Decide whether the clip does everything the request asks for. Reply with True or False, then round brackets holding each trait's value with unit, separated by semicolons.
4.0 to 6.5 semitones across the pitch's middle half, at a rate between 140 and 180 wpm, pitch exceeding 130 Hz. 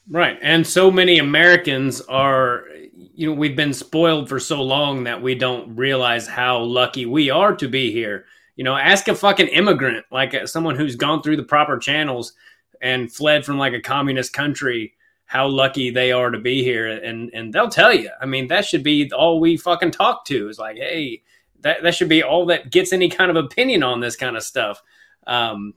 False (4.8 semitones; 205 wpm; 140 Hz)